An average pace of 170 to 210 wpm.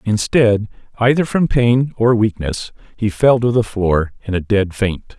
Yes: average, 175 wpm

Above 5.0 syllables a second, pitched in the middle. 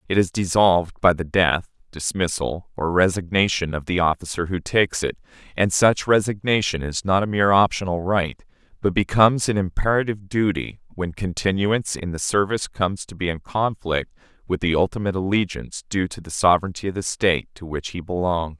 No: 5.7 syllables/s; very low, 95 Hz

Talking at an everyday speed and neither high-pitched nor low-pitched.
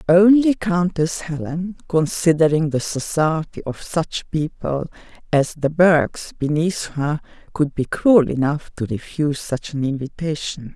No: slow, 130 wpm; medium, 160 Hz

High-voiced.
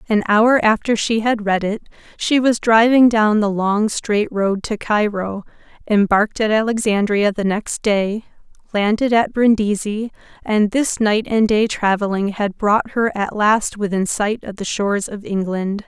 Yes: high, 210 Hz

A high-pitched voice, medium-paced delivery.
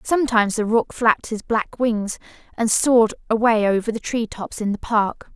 Yes: high, 225 Hz; average, 190 wpm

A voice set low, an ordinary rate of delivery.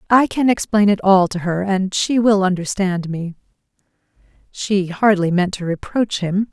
No: high, 195 Hz; average, 165 wpm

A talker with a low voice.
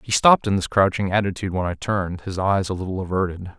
Yes: very low, 95 Hz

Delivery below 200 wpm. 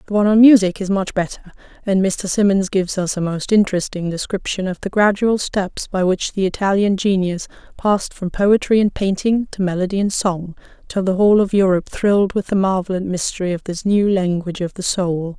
No: fast, 205 wpm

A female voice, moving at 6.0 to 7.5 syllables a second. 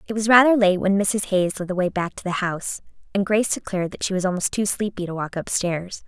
Yes: female; 6.1 syllables/s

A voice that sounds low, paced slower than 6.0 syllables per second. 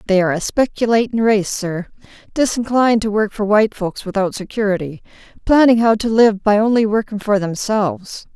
No: high, 210 Hz; 5.5 syllables/s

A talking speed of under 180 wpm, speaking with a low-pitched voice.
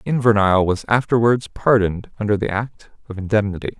Yes: average, 140 wpm; low, 105 Hz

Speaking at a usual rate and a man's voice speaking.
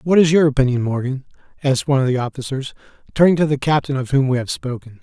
No: fast, 225 wpm; male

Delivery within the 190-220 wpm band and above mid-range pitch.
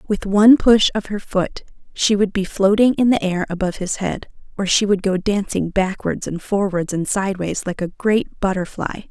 Yes: average, 200 wpm; high, 195 Hz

